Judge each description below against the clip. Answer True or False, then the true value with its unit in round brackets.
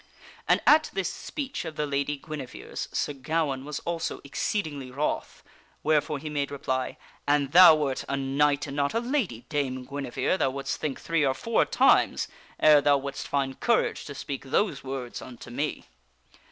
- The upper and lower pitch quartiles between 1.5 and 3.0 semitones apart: True (2.4 semitones)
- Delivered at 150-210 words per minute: True (175 wpm)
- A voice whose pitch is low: False (145 Hz)